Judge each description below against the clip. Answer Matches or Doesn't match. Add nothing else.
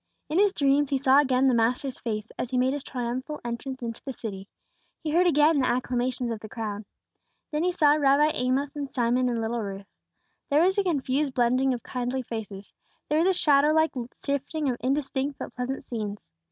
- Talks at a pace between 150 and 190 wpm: Doesn't match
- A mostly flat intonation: Doesn't match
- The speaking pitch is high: Matches